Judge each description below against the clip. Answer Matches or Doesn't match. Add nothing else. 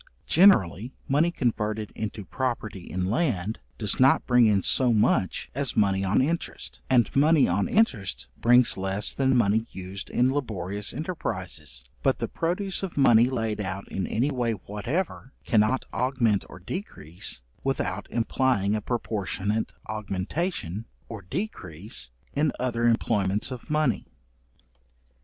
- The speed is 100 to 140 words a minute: Matches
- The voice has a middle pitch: Doesn't match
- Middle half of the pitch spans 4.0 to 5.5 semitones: Matches